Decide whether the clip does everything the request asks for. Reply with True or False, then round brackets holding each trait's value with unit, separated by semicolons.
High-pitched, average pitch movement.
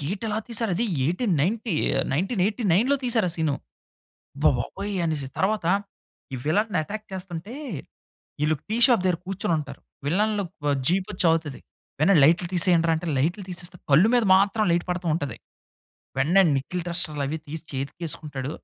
False (180 Hz; 4.6 semitones)